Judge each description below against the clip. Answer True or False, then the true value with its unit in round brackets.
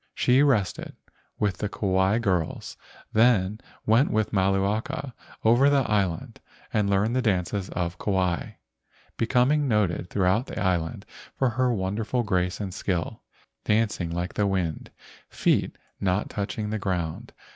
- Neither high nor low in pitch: False (100 Hz)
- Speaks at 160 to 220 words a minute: False (135 wpm)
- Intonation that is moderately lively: True (3.5 semitones)